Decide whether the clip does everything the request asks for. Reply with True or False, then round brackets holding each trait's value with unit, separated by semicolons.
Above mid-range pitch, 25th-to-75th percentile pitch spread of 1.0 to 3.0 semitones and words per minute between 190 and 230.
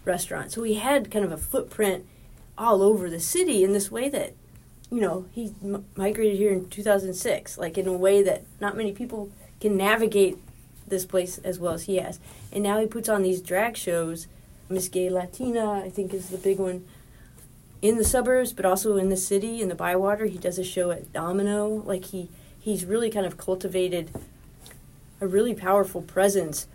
True (195 Hz; 2.5 semitones; 195 wpm)